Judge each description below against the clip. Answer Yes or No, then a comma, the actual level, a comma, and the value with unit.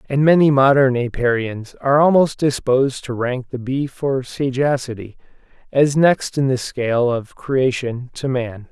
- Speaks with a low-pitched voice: Yes, low, 130 Hz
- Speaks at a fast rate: No, average, 150 wpm